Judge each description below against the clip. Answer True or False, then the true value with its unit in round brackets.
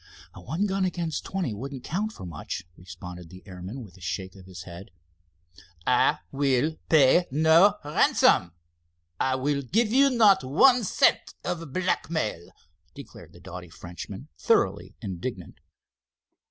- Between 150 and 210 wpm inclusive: False (135 wpm)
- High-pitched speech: False (130 Hz)